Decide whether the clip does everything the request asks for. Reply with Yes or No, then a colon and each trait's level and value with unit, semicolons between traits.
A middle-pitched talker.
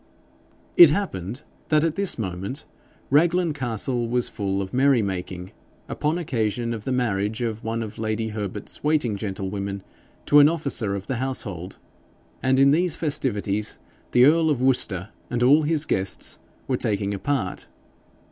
No: low, 120 Hz